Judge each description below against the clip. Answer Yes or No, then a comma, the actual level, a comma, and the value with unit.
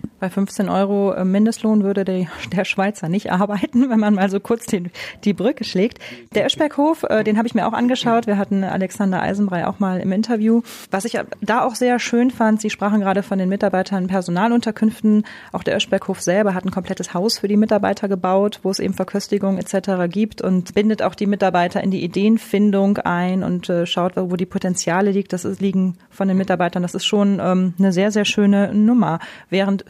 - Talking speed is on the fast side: Yes, fast, 200 wpm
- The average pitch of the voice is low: No, high, 200 Hz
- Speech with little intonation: Yes, narrow, 2.3 semitones